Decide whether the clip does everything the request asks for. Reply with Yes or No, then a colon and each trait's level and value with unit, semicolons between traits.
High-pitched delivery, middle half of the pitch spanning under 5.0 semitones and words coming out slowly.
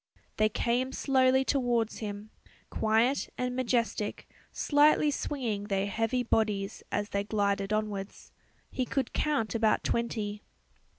Yes: high, 225 Hz; average, 3.7 semitones; slow, 120 wpm